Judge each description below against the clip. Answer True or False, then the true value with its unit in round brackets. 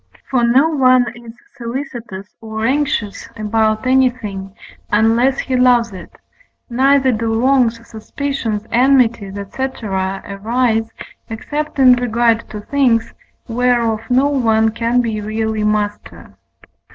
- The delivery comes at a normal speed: False (115 wpm)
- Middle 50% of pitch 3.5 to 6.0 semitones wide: False (2.7 semitones)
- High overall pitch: True (230 Hz)